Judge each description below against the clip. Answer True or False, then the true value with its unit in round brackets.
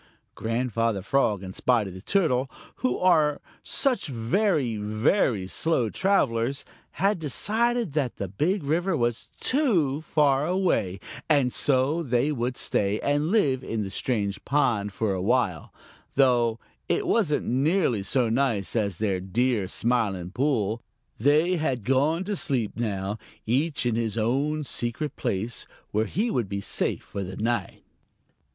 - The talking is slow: False (145 wpm)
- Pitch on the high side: False (125 Hz)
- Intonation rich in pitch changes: True (5.8 semitones)